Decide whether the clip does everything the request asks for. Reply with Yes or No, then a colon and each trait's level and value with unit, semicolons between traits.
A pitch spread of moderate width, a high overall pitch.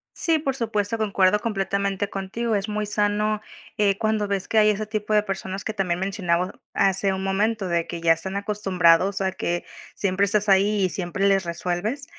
No: narrow, 1.9 semitones; high, 200 Hz